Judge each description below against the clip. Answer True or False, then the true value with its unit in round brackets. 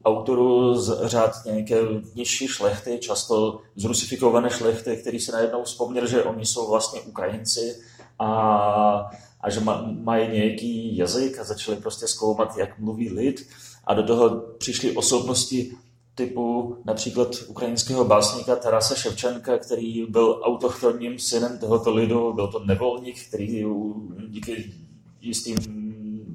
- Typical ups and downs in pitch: False (1.9 semitones)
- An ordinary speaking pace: True (125 wpm)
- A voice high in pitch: False (115 Hz)